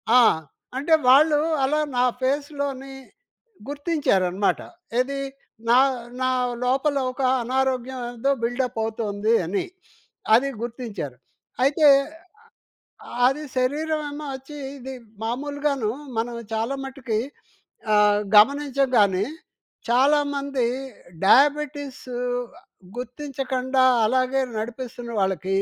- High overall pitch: Yes, very high, 260 Hz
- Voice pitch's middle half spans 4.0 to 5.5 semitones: No, average, 3.3 semitones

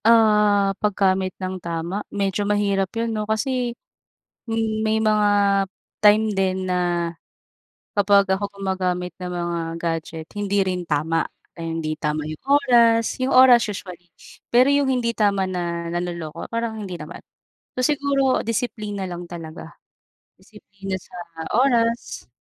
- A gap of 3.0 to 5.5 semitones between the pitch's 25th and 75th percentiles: Yes, average, 4.1 semitones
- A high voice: Yes, high, 200 Hz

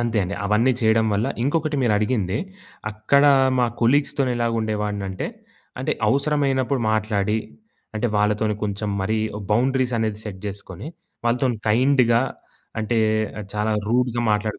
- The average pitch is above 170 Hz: No, low, 110 Hz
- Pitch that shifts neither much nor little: Yes, average, 3.2 semitones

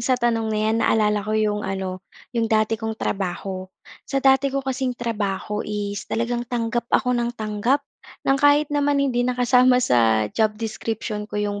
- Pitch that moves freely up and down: No, average, 3.1 semitones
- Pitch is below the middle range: No, high, 225 Hz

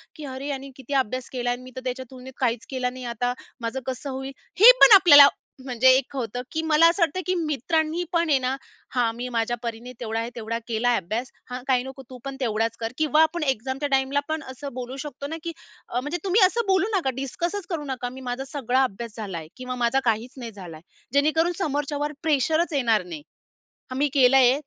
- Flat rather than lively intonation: No, average, 3.4 semitones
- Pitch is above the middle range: Yes, very high, 260 Hz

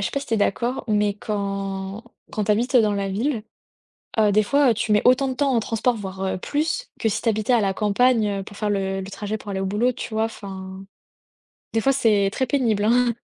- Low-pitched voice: No, high, 215 Hz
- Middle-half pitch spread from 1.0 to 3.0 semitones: No, average, 3.5 semitones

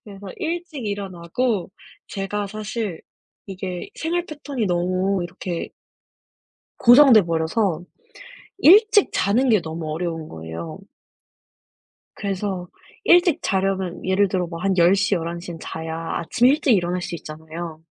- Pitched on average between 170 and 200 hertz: Yes, high, 190 Hz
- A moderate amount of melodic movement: Yes, average, 4.4 semitones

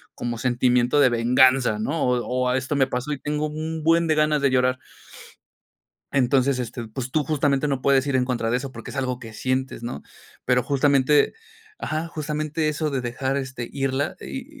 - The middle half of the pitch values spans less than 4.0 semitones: Yes, average, 3.0 semitones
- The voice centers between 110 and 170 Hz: Yes, low, 135 Hz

